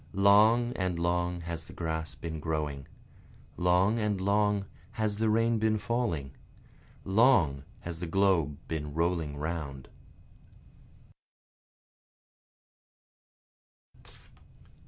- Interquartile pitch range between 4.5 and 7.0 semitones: Yes, average, 4.8 semitones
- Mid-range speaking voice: No, very low, 90 Hz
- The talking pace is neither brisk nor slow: No, slow, 95 wpm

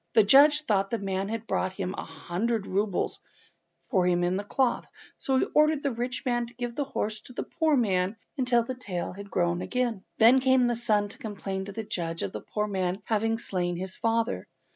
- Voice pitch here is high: Yes, high, 220 Hz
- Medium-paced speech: No, fast, 210 wpm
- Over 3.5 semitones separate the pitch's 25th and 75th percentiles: Yes, average, 4.4 semitones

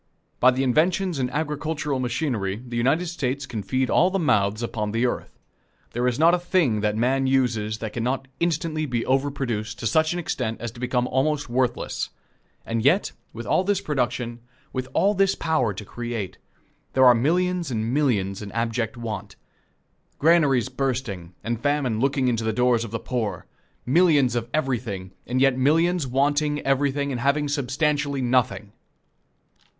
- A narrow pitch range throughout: No, average, 4.2 semitones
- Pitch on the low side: Yes, low, 130 Hz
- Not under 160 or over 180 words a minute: Yes, average, 170 wpm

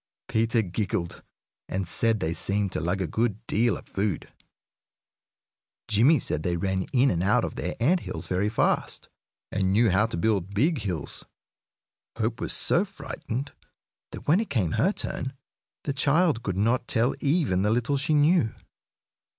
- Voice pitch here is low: Yes, low, 110 Hz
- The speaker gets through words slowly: No, average, 165 wpm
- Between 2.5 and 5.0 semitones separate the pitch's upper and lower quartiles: No, wide, 5.6 semitones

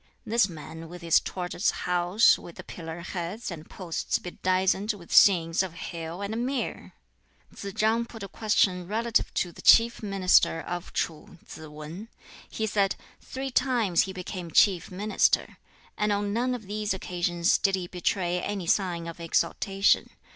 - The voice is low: No, medium, 185 Hz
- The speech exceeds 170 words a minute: No, average, 160 wpm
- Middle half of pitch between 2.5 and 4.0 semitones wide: Yes, average, 3.5 semitones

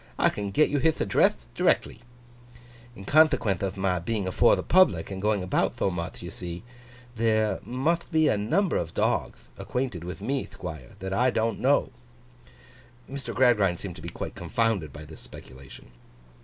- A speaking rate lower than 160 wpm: No, average, 170 wpm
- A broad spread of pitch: Yes, wide, 6.2 semitones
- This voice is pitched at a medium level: No, low, 100 Hz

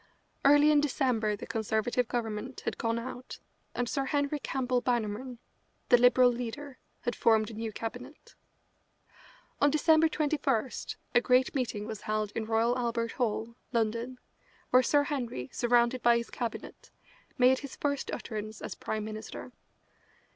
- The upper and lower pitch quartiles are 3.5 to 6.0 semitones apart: No, average, 2.8 semitones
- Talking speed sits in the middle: Yes, average, 145 wpm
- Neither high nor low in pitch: No, high, 245 Hz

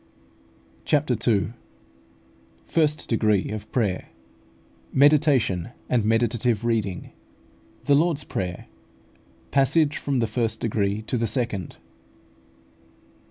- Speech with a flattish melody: No, average, 4.5 semitones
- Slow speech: Yes, slow, 95 wpm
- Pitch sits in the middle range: No, low, 115 Hz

